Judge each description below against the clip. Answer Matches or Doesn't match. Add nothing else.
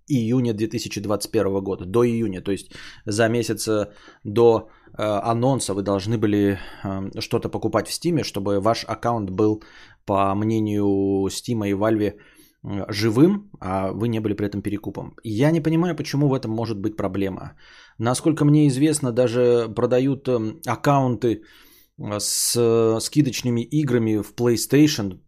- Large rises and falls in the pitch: Doesn't match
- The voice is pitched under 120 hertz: Matches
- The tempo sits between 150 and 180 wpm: Doesn't match